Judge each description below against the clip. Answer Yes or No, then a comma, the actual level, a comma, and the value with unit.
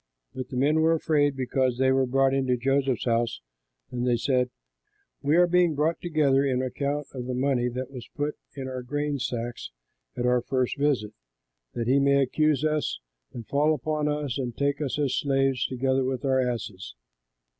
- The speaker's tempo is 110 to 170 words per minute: No, average, 185 wpm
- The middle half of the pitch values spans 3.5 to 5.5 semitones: No, narrow, 2.5 semitones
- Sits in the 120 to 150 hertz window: Yes, low, 135 Hz